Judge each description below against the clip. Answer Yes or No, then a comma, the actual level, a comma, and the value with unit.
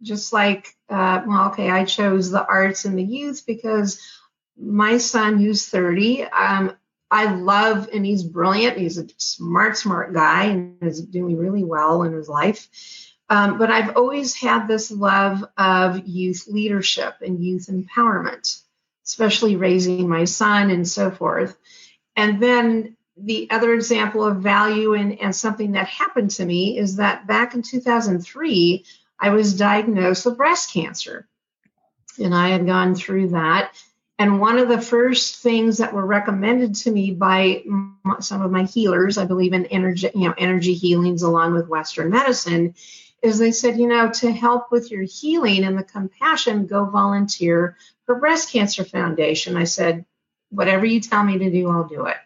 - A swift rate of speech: No, average, 165 wpm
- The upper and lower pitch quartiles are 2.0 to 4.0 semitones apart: Yes, average, 3.4 semitones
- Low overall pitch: No, high, 200 Hz